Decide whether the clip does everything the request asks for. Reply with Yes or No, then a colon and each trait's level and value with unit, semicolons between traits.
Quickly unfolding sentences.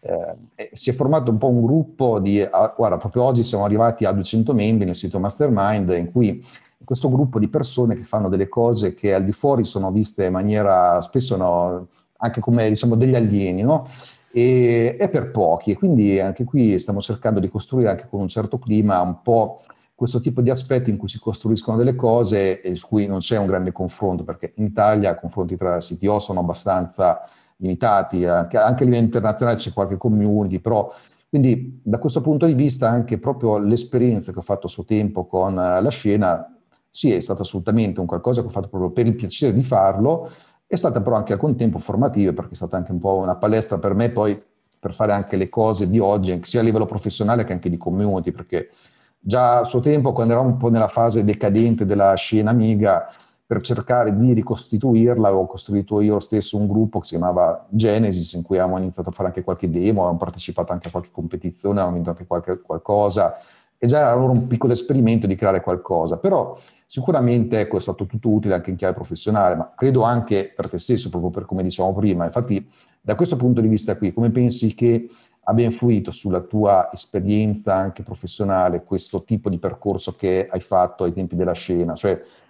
Yes: fast, 205 wpm